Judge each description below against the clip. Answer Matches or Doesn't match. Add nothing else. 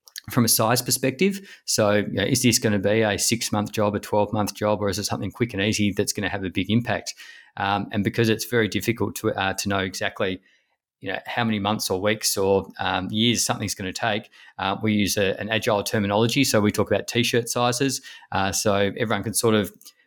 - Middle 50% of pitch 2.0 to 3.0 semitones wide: Matches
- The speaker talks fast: Matches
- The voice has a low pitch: Matches